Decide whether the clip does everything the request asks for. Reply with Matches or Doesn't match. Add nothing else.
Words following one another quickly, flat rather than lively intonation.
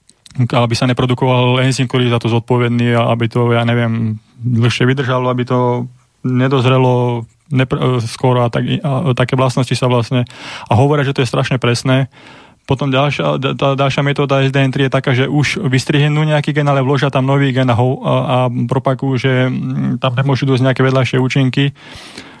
Matches